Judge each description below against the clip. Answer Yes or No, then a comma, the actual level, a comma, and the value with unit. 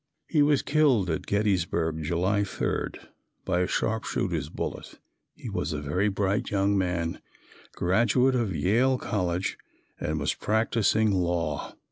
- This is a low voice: Yes, very low, 95 Hz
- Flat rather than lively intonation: No, average, 4.1 semitones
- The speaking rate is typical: No, slow, 130 wpm